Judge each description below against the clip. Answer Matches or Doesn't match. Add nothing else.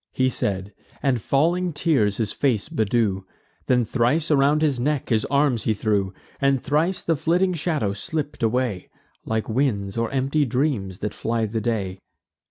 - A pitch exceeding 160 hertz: Doesn't match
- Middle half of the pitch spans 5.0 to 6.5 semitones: Matches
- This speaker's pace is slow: Doesn't match